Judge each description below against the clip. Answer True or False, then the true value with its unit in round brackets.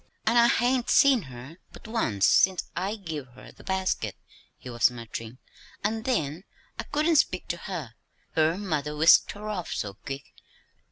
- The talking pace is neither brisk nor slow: True (165 wpm)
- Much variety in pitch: True (8.0 semitones)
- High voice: False (175 Hz)